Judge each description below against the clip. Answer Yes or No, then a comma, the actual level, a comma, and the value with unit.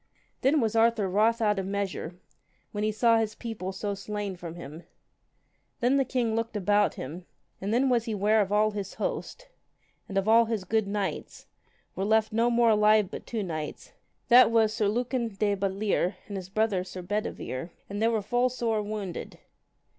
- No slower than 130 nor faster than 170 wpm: No, average, 185 wpm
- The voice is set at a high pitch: Yes, high, 210 Hz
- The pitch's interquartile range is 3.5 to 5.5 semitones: No, average, 2.7 semitones